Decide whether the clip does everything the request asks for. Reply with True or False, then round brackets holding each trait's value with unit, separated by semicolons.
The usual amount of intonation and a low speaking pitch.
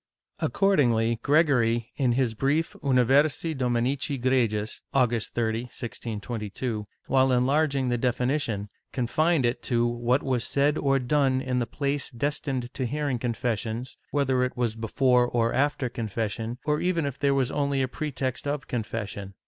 True (3.1 semitones; 125 Hz)